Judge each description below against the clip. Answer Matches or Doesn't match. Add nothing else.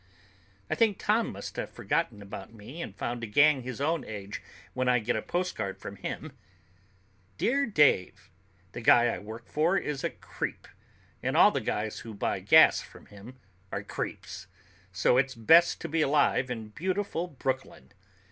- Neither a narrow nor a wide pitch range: Doesn't match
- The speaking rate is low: Doesn't match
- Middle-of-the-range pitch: Doesn't match